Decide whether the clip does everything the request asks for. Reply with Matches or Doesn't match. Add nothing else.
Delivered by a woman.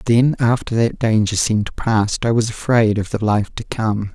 Doesn't match